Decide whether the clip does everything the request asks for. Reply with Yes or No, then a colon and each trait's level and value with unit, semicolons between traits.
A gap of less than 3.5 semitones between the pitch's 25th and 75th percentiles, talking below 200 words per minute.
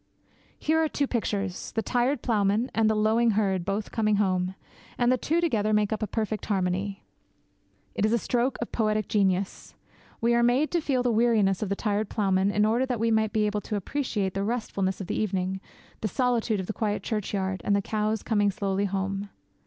No: average, 2.9 semitones; fast, 205 wpm